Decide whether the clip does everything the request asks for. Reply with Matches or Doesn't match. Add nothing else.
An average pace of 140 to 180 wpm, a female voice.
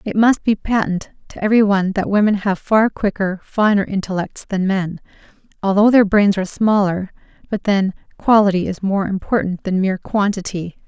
Matches